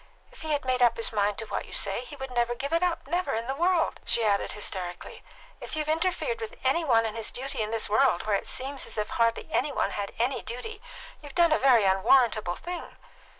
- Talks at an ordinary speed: No, fast, 235 wpm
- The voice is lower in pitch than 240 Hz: No, very high, 250 Hz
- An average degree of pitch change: No, wide, 5.9 semitones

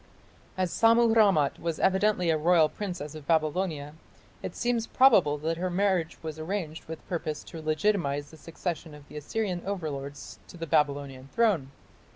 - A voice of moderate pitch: Yes, medium, 165 Hz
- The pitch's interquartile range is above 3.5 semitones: Yes, average, 4.3 semitones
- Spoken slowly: No, average, 160 wpm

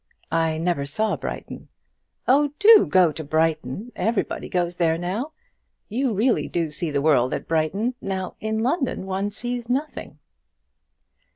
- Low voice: No, high, 190 Hz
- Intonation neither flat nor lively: No, wide, 6.9 semitones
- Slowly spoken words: No, average, 145 wpm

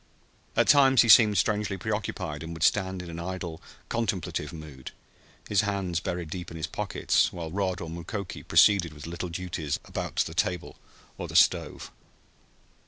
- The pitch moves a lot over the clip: No, average, 3.5 semitones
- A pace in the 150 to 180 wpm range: Yes, average, 170 wpm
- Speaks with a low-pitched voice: Yes, very low, 90 Hz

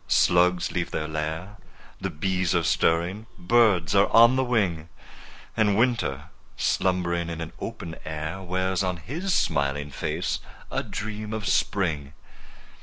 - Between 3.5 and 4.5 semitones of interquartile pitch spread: Yes, average, 4.2 semitones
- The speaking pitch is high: No, very low, 90 Hz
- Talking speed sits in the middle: No, slow, 130 wpm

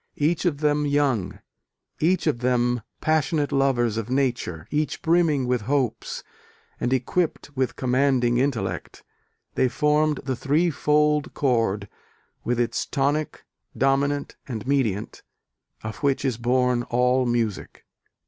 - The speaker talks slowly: Yes, slow, 125 wpm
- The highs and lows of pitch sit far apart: No, average, 3.3 semitones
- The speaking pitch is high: No, low, 130 Hz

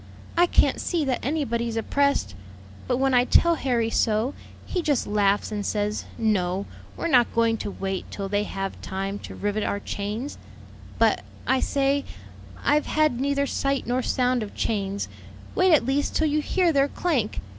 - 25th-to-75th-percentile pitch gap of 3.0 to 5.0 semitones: No, wide, 5.4 semitones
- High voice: Yes, high, 245 Hz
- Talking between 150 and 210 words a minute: Yes, average, 170 wpm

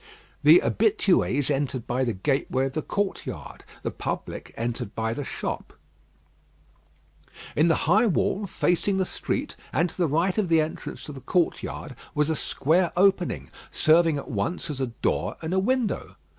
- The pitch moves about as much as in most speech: No, wide, 5.7 semitones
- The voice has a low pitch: No, medium, 160 Hz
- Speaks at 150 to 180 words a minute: Yes, average, 165 wpm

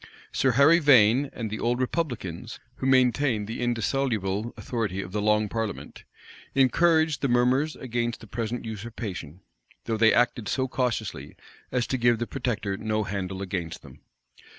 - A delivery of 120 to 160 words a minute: Yes, average, 150 wpm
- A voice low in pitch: Yes, low, 120 Hz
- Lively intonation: No, average, 3.5 semitones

